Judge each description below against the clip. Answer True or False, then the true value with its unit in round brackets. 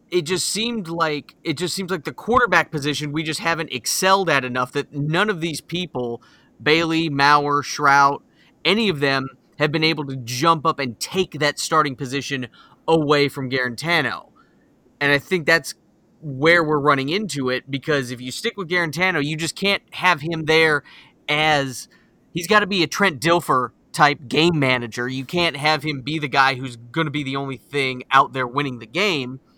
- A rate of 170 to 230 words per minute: True (190 wpm)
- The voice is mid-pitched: True (150 Hz)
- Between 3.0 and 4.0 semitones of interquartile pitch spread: True (3.5 semitones)